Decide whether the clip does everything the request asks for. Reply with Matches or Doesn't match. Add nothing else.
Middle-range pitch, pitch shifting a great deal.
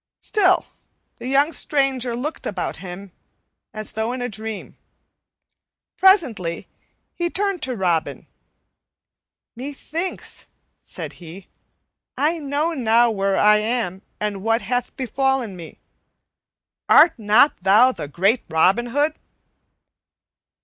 Doesn't match